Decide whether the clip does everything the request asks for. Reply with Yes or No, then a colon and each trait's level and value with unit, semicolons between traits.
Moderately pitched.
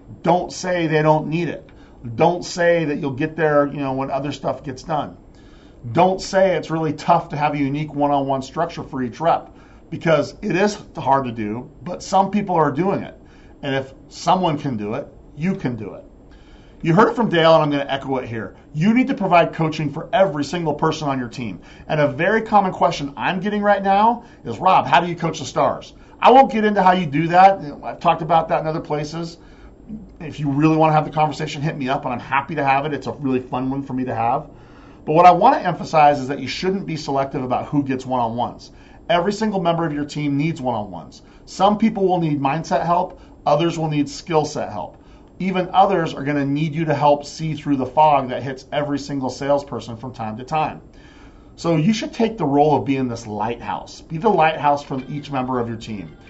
Yes: medium, 150 Hz